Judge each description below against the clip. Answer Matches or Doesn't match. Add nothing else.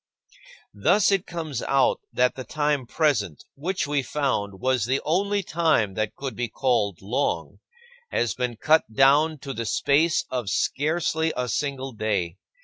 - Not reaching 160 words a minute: Matches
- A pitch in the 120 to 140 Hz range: Matches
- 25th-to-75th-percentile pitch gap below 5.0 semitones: Doesn't match